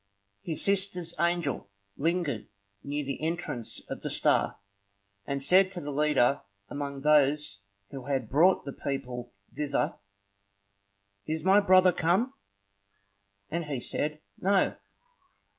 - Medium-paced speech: No, slow, 120 wpm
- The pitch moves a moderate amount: Yes, average, 4.2 semitones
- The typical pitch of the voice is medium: Yes, medium, 150 Hz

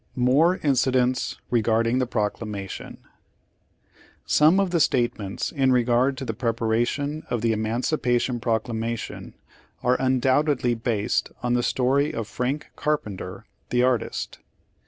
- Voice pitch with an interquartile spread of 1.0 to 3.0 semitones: Yes, narrow, 2.6 semitones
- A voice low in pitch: Yes, low, 125 Hz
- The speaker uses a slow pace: Yes, slow, 125 wpm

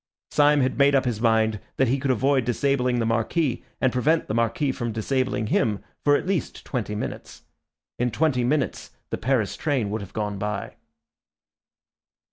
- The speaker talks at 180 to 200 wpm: No, average, 170 wpm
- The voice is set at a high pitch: No, low, 125 Hz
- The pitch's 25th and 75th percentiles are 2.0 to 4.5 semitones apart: Yes, average, 4.0 semitones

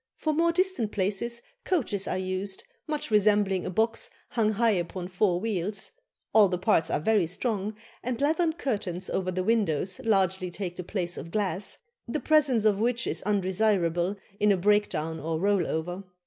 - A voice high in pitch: Yes, high, 200 Hz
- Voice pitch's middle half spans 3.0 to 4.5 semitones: Yes, average, 3.6 semitones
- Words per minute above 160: Yes, average, 175 wpm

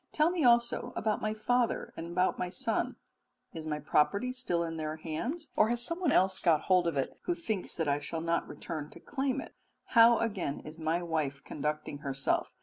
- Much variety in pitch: Yes, wide, 7.2 semitones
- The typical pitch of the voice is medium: Yes, medium, 180 Hz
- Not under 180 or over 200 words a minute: Yes, average, 195 wpm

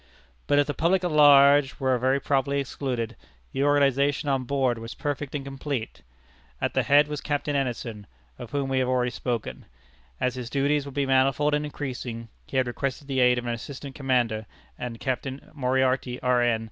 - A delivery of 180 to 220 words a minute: Yes, average, 185 wpm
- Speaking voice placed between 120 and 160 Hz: Yes, low, 135 Hz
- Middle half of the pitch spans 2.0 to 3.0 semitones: Yes, narrow, 2.4 semitones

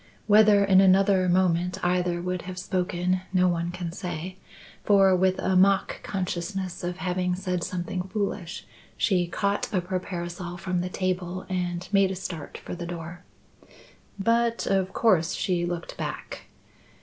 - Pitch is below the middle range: No, medium, 185 Hz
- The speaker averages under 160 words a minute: Yes, average, 150 wpm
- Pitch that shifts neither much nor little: No, narrow, 1.5 semitones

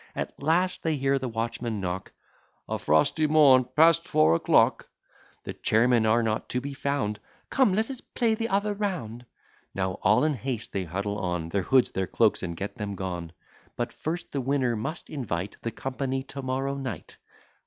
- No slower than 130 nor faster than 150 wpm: No, average, 180 wpm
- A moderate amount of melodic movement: No, wide, 6.3 semitones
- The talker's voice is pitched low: Yes, low, 125 Hz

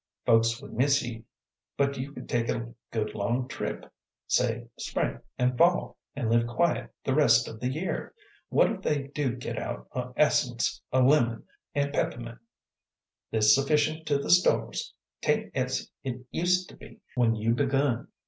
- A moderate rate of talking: Yes, average, 165 wpm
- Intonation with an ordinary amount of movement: Yes, average, 3.6 semitones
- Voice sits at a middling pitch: No, low, 125 Hz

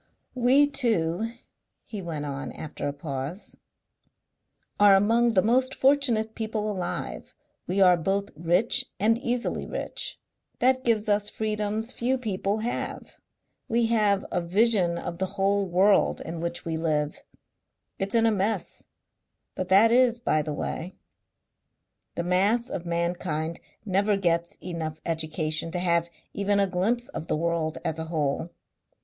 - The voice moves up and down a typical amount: Yes, average, 4.8 semitones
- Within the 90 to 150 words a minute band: Yes, average, 145 wpm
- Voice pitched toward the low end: No, high, 195 Hz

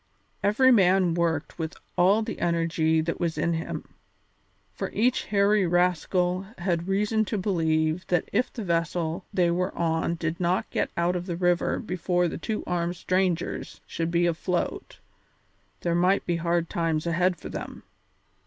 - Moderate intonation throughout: No, narrow, 1.9 semitones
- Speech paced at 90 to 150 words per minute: No, average, 160 wpm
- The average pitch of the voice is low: No, medium, 175 Hz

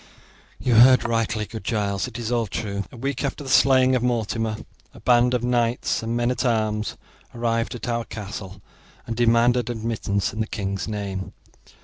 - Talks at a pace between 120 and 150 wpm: No, average, 175 wpm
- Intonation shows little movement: Yes, narrow, 2.2 semitones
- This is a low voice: Yes, low, 115 Hz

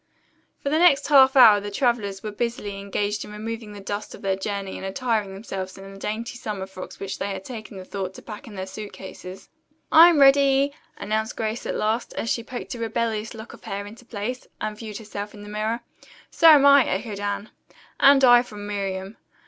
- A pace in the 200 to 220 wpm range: Yes, fast, 205 wpm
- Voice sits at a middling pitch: No, high, 215 Hz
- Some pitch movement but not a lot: Yes, average, 3.2 semitones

